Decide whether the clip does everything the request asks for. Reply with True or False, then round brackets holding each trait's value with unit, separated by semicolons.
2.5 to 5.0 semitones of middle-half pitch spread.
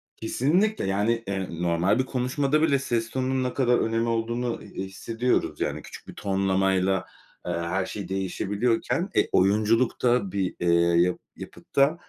True (4.7 semitones)